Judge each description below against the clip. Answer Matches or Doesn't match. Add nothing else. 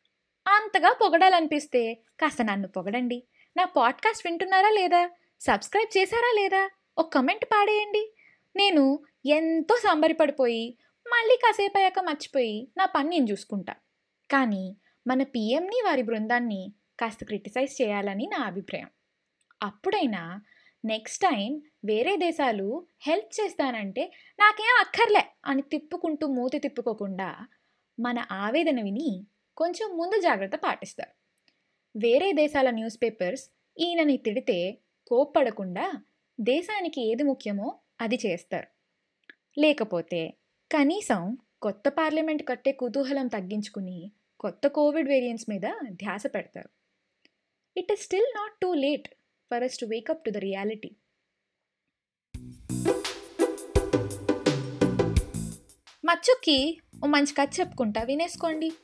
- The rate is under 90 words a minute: Doesn't match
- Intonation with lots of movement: Matches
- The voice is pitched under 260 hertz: Doesn't match